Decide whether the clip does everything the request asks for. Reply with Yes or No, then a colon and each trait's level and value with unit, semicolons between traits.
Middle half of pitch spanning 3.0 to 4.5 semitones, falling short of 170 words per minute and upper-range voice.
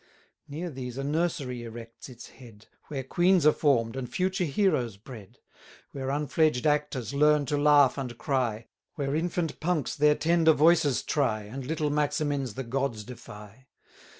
No: average, 3.6 semitones; average, 150 wpm; medium, 140 Hz